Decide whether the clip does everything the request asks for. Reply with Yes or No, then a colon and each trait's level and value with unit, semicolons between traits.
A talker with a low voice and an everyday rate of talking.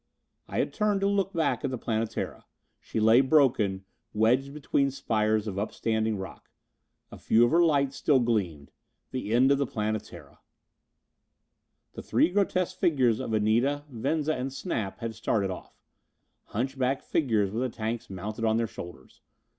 Yes: low, 120 Hz; average, 155 wpm